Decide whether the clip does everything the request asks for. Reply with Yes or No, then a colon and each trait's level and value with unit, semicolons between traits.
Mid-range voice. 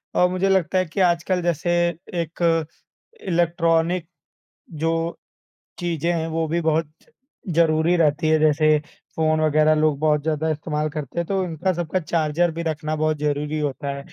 Yes: medium, 160 Hz